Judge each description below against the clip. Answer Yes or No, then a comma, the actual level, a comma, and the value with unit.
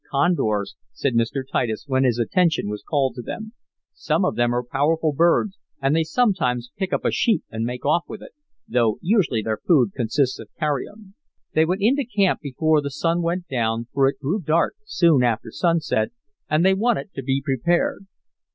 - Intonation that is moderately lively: No, wide, 6.3 semitones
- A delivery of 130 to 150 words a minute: No, average, 190 wpm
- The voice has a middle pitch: Yes, medium, 150 Hz